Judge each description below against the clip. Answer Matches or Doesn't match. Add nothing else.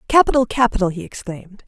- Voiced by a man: Doesn't match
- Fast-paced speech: Doesn't match